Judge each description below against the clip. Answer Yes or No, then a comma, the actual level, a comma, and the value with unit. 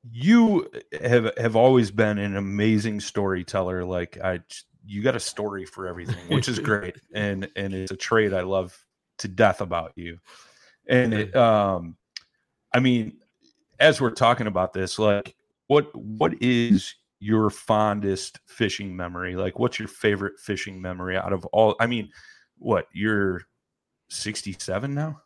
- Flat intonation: No, average, 3.6 semitones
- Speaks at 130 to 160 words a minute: Yes, average, 150 wpm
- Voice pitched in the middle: No, low, 105 Hz